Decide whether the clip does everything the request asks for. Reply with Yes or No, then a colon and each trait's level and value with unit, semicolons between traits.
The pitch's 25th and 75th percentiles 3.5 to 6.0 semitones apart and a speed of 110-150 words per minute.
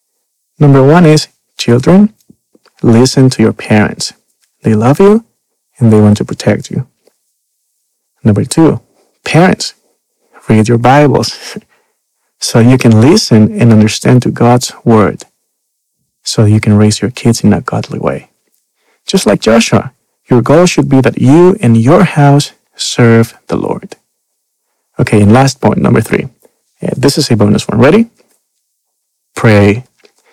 Yes: average, 5.0 semitones; average, 140 wpm